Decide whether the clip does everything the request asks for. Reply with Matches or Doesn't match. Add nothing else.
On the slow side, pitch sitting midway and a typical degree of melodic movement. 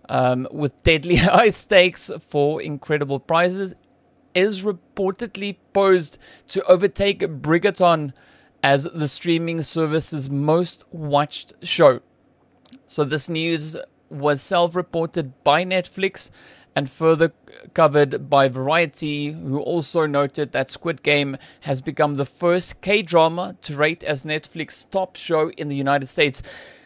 Matches